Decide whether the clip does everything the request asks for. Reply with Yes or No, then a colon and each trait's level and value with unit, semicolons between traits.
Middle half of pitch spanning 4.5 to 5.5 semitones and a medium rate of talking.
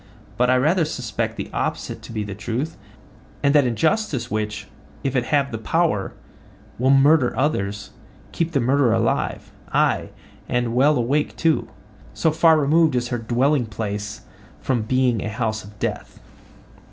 Yes: average, 4.8 semitones; average, 150 wpm